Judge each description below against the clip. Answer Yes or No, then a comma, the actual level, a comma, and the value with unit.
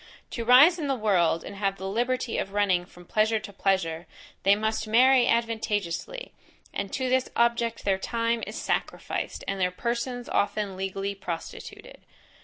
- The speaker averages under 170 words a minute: Yes, average, 160 wpm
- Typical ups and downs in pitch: Yes, average, 3.4 semitones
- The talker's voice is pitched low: No, high, 215 Hz